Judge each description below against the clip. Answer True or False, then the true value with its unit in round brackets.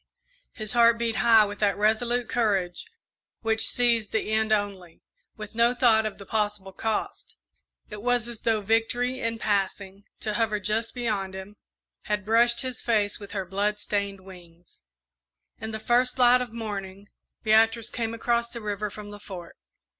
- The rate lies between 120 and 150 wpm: False (165 wpm)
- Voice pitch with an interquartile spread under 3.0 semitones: True (2.4 semitones)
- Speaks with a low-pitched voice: False (215 Hz)